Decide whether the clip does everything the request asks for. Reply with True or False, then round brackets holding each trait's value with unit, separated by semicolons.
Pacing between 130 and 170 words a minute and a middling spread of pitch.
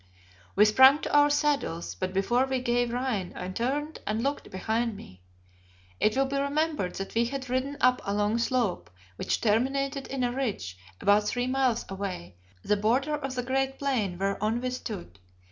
False (180 wpm; 4.7 semitones)